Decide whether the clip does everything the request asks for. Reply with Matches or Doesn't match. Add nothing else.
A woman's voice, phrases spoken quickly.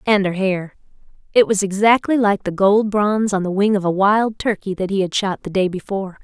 Matches